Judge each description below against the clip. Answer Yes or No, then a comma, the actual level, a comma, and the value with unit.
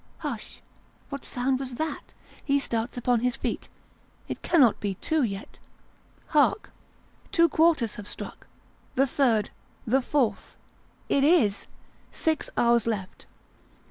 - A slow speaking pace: Yes, slow, 125 wpm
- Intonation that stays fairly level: No, average, 4.1 semitones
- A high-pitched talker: Yes, very high, 250 Hz